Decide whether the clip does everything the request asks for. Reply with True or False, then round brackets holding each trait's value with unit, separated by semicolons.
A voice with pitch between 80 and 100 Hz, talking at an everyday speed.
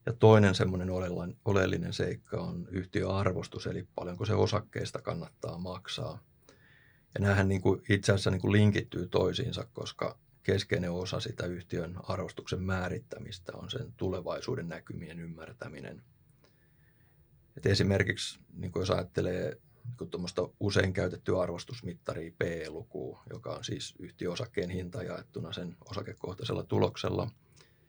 True (95 Hz; 115 wpm)